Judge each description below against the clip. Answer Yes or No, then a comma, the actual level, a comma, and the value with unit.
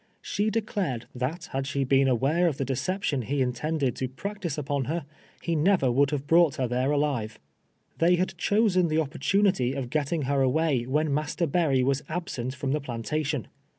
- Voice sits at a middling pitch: Yes, medium, 145 Hz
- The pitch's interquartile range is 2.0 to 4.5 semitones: Yes, average, 4.2 semitones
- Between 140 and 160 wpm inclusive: No, average, 175 wpm